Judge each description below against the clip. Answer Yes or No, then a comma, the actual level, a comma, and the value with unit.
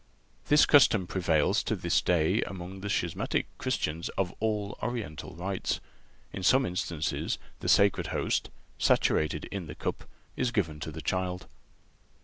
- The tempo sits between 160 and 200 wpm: No, average, 140 wpm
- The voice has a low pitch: Yes, very low, 90 Hz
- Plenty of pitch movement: No, average, 3.9 semitones